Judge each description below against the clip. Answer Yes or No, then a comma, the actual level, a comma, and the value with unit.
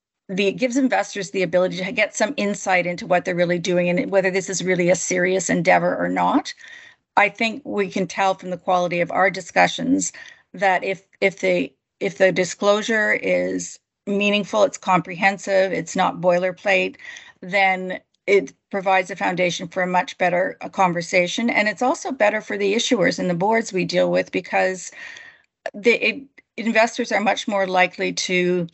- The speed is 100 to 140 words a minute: No, average, 170 wpm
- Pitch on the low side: No, high, 195 Hz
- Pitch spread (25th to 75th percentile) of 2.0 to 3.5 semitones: Yes, average, 3.1 semitones